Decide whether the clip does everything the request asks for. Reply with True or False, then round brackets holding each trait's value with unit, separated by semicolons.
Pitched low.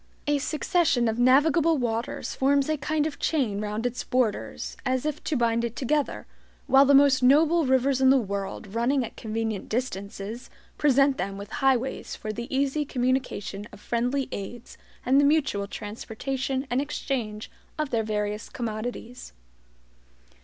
False (250 Hz)